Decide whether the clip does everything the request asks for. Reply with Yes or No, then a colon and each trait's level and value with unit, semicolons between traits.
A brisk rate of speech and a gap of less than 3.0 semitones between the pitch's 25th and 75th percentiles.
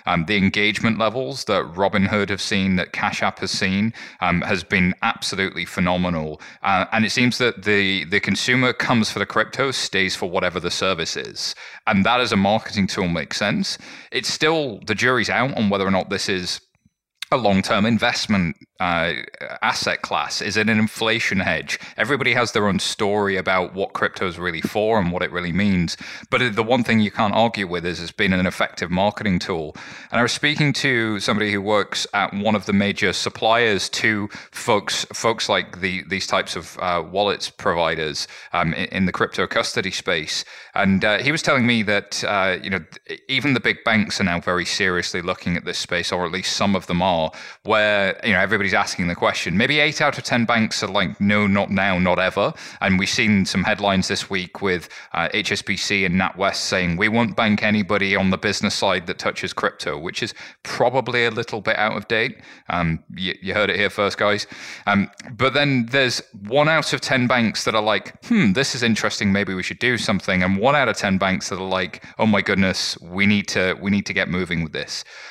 No: fast, 210 wpm; average, 3.5 semitones